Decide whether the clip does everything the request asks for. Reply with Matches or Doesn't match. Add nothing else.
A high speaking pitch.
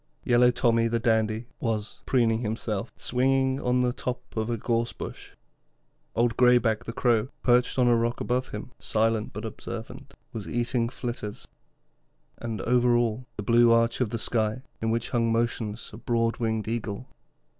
Doesn't match